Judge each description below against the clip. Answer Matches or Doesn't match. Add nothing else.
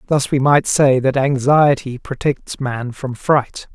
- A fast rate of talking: Doesn't match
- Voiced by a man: Matches